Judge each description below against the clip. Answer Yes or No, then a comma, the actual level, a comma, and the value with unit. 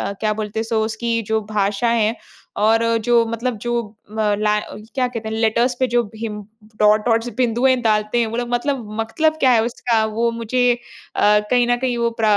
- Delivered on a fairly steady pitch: Yes, narrow, 1.7 semitones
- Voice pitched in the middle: No, high, 230 Hz